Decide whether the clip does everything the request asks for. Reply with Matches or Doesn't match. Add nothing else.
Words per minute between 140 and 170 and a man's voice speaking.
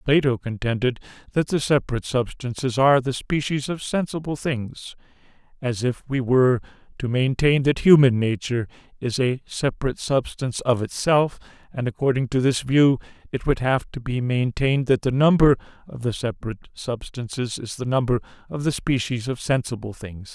Matches